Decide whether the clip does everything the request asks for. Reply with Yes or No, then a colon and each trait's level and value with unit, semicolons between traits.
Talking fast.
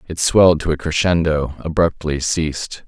No: average, 145 wpm